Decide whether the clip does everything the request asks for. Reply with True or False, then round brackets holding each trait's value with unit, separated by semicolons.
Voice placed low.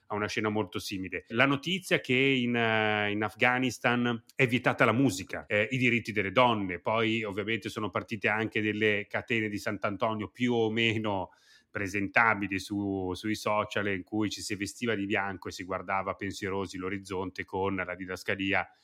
True (105 Hz)